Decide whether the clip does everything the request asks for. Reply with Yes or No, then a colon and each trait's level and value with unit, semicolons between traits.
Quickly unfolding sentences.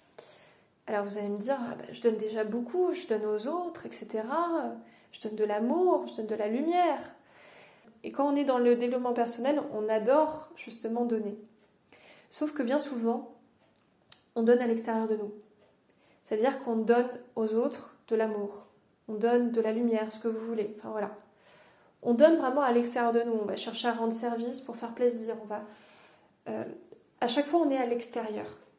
No: average, 190 wpm